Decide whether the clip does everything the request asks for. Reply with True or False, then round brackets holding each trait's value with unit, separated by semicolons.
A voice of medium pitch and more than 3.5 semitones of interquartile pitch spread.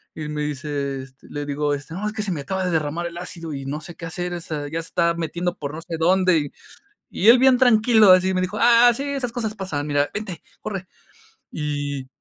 True (170 Hz; 4.7 semitones)